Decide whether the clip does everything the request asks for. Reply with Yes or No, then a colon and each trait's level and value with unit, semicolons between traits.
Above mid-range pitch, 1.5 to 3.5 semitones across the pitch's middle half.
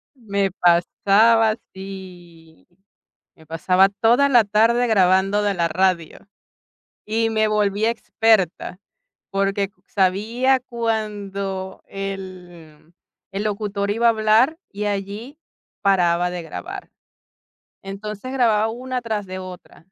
Yes: high, 200 Hz; average, 3.0 semitones